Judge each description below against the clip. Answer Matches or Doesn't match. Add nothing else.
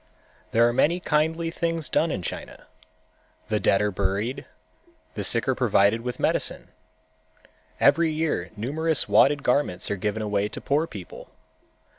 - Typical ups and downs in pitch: Doesn't match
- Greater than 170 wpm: Doesn't match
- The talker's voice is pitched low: Matches